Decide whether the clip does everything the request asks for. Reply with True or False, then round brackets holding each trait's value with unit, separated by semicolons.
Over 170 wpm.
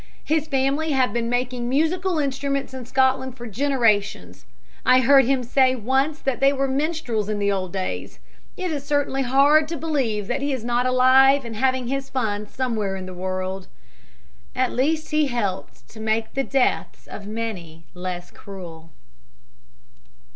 False (160 wpm)